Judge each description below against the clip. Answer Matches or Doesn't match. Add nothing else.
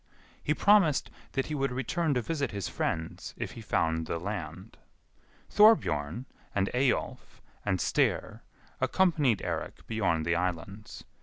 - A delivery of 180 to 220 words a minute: Doesn't match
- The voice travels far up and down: Matches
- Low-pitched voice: Matches